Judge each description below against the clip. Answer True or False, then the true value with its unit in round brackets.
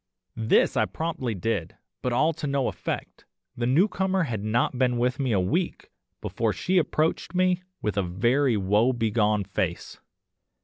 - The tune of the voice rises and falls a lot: True (6.4 semitones)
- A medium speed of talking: True (160 wpm)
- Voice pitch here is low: True (125 Hz)